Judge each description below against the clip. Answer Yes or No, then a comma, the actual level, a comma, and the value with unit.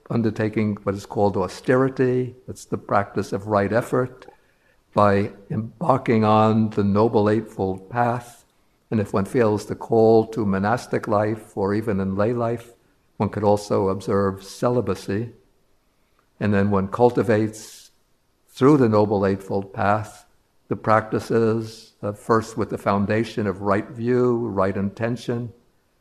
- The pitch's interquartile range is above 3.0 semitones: No, average, 2.7 semitones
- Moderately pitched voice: No, low, 110 Hz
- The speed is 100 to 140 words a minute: Yes, slow, 135 wpm